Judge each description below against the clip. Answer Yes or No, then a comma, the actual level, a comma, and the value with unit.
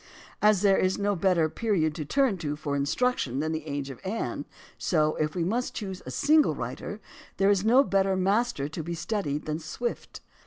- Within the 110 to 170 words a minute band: No, average, 200 wpm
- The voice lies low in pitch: No, medium, 180 Hz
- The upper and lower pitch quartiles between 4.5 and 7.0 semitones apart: Yes, average, 5.3 semitones